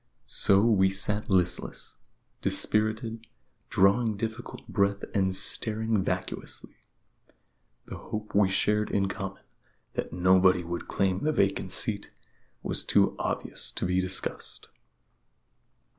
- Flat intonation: Yes, narrow, 2.3 semitones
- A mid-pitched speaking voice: No, low, 100 Hz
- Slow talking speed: Yes, slow, 115 wpm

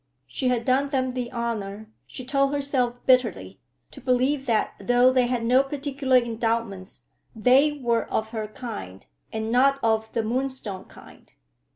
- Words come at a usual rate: Yes, average, 155 wpm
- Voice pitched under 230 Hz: No, high, 245 Hz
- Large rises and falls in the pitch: No, average, 2.8 semitones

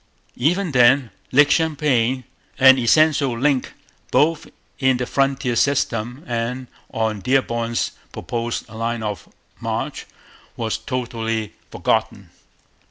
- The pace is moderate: No, slow, 100 wpm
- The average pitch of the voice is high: No, low, 125 Hz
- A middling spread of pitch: Yes, average, 3.1 semitones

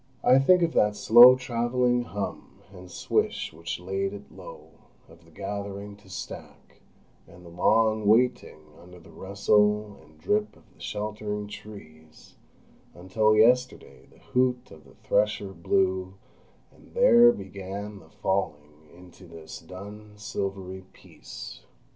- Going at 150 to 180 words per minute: No, slow, 135 wpm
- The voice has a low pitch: Yes, low, 100 Hz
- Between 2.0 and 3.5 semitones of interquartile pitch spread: Yes, average, 2.9 semitones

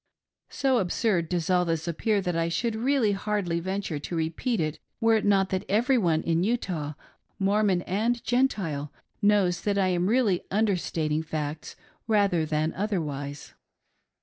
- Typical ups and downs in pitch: Yes, average, 4.4 semitones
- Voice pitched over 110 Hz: Yes, medium, 185 Hz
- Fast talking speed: No, average, 160 wpm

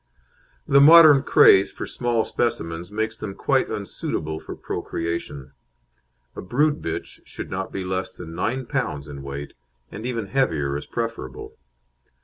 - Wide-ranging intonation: Yes, wide, 7.5 semitones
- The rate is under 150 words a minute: Yes, average, 140 wpm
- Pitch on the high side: No, very low, 95 Hz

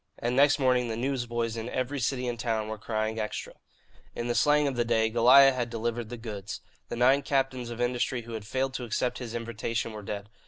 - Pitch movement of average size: No, narrow, 2.3 semitones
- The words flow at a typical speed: No, fast, 220 wpm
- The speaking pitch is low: Yes, low, 120 Hz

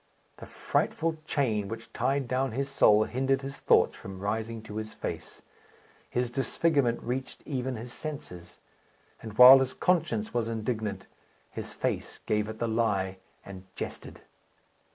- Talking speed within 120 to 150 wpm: Yes, average, 145 wpm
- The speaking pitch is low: Yes, low, 115 Hz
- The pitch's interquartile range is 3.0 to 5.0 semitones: Yes, average, 3.8 semitones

